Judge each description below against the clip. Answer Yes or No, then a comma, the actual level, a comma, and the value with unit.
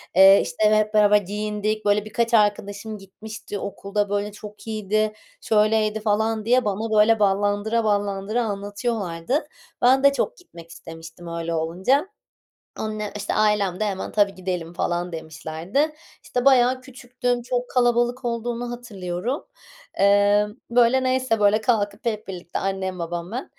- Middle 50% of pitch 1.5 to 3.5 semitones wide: Yes, average, 3.1 semitones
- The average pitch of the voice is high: Yes, high, 210 Hz